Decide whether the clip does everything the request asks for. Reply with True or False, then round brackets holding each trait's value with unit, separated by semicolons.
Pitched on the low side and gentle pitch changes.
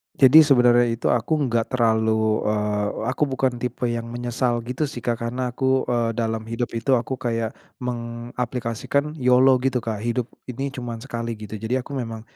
True (120 Hz; 1.9 semitones)